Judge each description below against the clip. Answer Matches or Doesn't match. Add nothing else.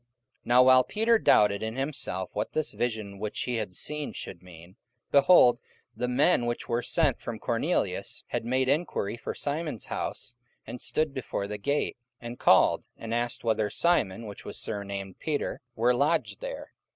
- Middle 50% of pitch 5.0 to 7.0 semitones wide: Matches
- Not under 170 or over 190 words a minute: Matches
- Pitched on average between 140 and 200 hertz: Doesn't match